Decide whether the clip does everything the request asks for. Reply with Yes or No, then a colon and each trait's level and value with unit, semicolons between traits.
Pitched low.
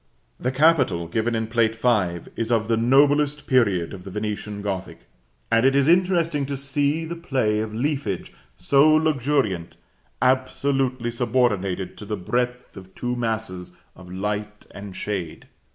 Yes: low, 115 Hz